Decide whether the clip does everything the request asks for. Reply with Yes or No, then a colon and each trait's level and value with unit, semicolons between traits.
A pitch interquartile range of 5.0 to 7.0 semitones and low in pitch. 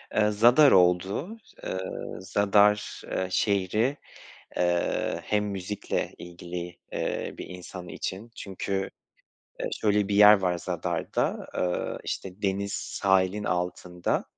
No: narrow, 2.6 semitones; very low, 95 Hz